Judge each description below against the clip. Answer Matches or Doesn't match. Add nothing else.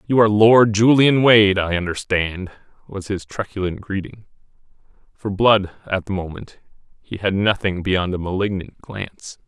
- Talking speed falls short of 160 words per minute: Matches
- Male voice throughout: Matches